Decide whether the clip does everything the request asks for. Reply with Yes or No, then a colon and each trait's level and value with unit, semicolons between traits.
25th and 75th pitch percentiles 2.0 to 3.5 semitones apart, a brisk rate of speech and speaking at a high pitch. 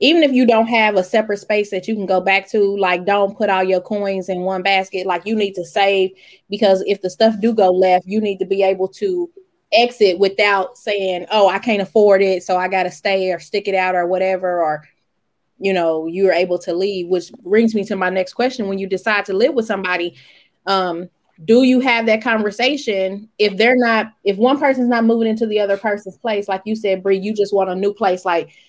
Yes: narrow, 2.6 semitones; fast, 230 wpm; high, 195 Hz